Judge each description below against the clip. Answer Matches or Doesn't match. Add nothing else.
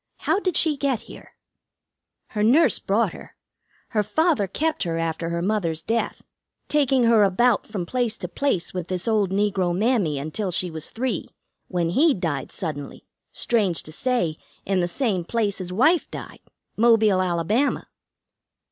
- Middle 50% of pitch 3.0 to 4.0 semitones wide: Doesn't match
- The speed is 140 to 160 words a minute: Matches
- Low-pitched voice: Doesn't match